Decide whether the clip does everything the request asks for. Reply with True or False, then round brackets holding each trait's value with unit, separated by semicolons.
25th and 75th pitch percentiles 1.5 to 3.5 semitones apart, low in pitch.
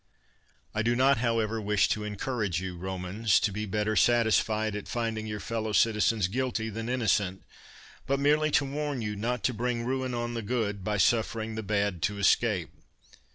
True (2.6 semitones; 110 Hz)